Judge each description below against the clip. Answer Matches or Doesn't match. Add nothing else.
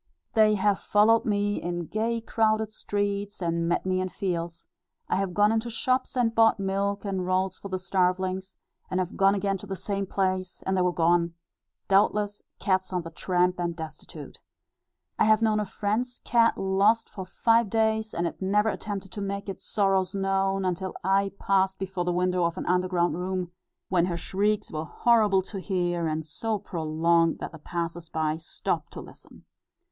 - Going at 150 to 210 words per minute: Matches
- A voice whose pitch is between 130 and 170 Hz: Doesn't match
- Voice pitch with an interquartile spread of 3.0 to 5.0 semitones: Doesn't match